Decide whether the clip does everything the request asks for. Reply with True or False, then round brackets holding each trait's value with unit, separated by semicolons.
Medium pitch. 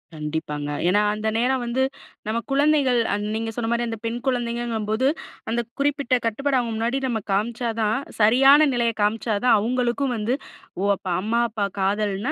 False (235 Hz)